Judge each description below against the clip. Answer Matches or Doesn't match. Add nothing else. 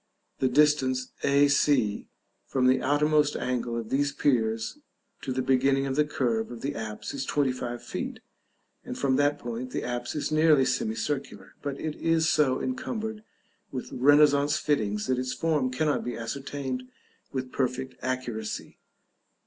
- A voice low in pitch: Matches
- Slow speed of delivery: Doesn't match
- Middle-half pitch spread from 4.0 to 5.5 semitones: Doesn't match